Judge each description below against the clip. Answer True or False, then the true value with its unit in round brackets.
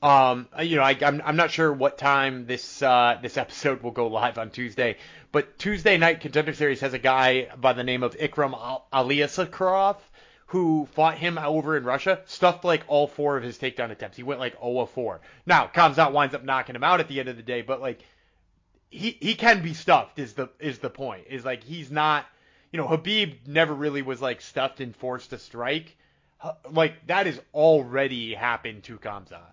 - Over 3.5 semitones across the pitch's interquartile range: True (4.0 semitones)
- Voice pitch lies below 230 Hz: True (140 Hz)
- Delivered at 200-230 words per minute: True (205 wpm)